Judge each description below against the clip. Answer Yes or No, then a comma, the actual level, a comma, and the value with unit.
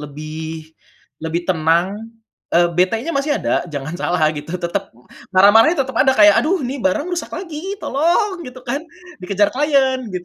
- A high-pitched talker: Yes, high, 205 Hz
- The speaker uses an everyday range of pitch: No, wide, 8.5 semitones